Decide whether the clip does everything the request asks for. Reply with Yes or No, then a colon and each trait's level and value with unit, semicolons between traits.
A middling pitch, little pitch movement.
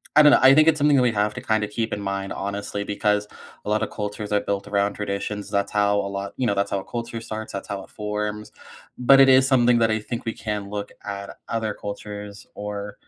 No: low, 105 Hz; narrow, 2.1 semitones